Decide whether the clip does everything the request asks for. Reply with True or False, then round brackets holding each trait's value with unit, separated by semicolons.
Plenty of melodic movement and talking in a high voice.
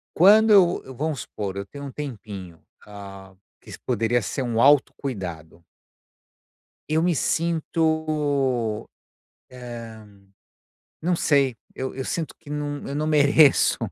False (5.8 semitones; 135 Hz)